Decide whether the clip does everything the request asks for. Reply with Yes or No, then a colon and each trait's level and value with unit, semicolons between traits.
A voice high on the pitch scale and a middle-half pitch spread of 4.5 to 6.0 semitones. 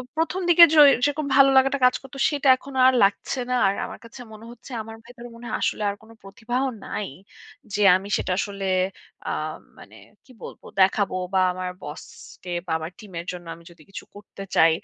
Yes: high, 220 Hz; wide, 5.4 semitones